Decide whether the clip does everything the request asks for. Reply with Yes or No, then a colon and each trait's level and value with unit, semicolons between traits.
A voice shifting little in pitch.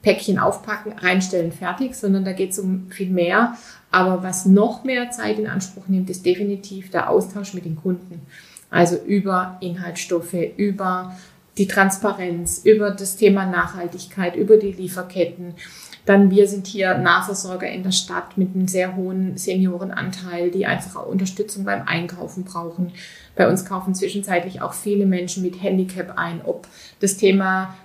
Yes: narrow, 1.7 semitones